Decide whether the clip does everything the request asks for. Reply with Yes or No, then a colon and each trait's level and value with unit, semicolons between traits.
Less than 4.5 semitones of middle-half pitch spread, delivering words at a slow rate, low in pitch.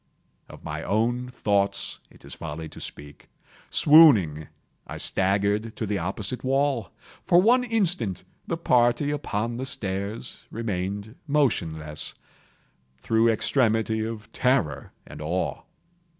No: average, 4.9 semitones; slow, 120 wpm; low, 110 Hz